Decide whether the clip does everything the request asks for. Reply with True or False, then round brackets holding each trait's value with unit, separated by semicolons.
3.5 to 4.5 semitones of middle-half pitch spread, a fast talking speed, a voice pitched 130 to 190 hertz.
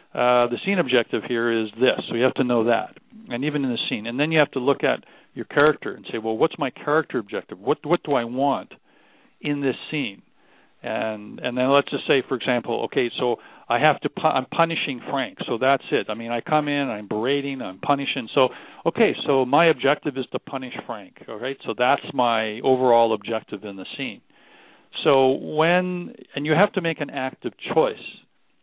True (3.8 semitones; 210 wpm; 135 Hz)